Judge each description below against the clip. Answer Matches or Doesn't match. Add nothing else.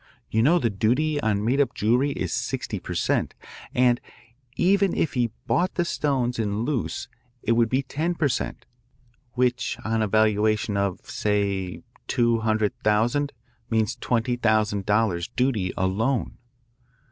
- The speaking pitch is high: Doesn't match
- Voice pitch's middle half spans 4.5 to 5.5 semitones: Doesn't match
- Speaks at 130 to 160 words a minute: Matches